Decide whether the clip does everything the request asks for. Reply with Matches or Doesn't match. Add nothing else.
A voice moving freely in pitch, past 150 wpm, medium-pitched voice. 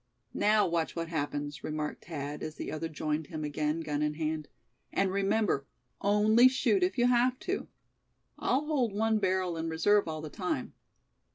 Matches